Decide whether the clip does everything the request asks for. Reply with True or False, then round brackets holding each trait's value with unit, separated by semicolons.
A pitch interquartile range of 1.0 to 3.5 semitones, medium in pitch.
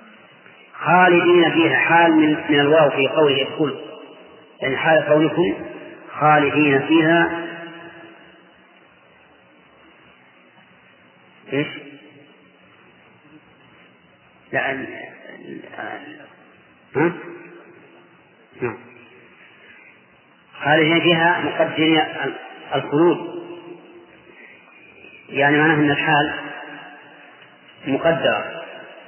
True (2.4 semitones; 155 Hz)